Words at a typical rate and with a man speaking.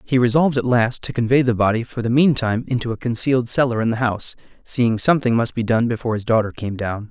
No: fast, 235 wpm; male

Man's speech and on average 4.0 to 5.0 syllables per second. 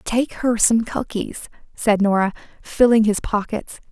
No: female; 4.1 syllables/s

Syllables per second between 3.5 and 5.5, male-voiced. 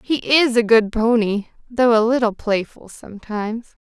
No: 4.6 syllables/s; female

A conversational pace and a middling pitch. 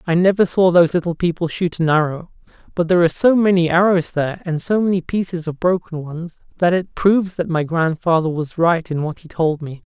No: fast, 220 wpm; medium, 170 Hz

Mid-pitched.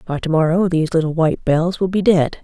Yes: medium, 170 Hz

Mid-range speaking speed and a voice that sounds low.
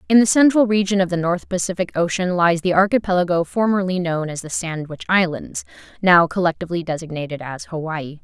No: average, 165 wpm; medium, 180 Hz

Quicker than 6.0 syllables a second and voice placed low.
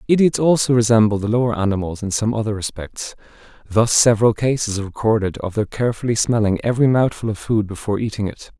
Yes: 6.5 syllables/s; low, 110 Hz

